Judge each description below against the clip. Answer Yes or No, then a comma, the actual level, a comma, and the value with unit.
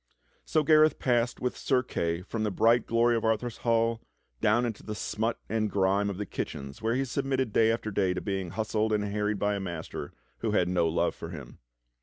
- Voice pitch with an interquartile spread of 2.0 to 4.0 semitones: Yes, average, 3.0 semitones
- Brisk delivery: Yes, fast, 210 wpm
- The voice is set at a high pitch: No, low, 110 Hz